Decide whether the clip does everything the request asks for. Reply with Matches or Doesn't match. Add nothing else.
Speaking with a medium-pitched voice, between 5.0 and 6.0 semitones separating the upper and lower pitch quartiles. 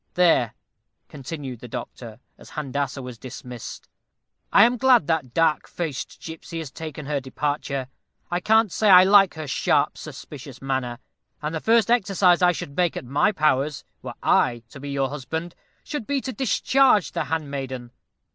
Matches